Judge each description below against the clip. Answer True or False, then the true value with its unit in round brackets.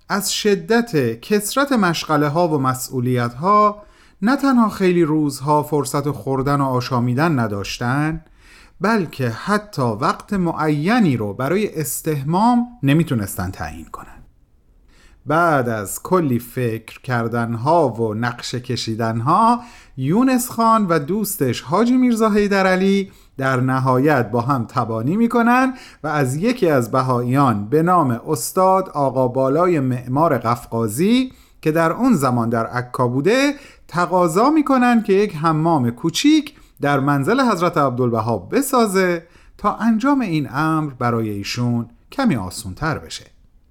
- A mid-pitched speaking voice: True (150 Hz)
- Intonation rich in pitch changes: True (8.5 semitones)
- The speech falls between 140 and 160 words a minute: False (120 wpm)